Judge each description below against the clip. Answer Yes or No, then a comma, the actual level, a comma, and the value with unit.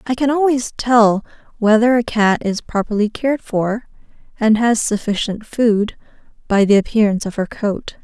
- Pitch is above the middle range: Yes, high, 225 Hz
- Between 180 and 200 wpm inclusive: No, average, 155 wpm